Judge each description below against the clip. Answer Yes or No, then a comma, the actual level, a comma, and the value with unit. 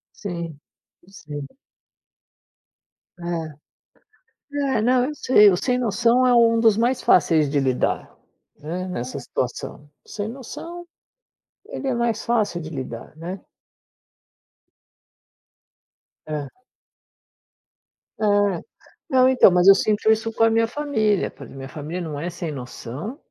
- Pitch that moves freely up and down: Yes, wide, 7.2 semitones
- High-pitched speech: Yes, high, 200 Hz